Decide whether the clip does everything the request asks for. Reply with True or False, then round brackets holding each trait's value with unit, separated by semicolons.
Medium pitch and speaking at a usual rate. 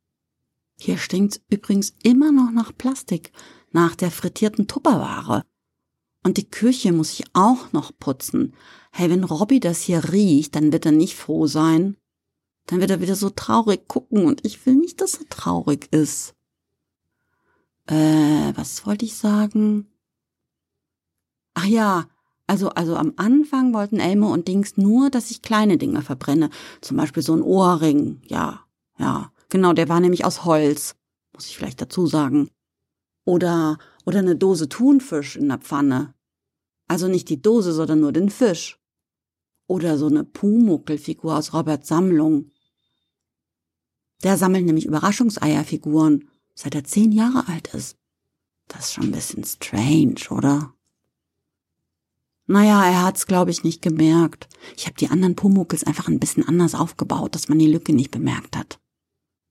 True (170 Hz; 150 wpm)